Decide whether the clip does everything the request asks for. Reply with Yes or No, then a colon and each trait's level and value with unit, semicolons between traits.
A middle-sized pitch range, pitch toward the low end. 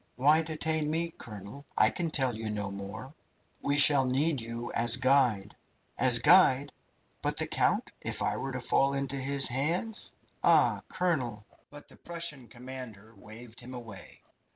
Yes: average, 4.1 semitones; low, 130 Hz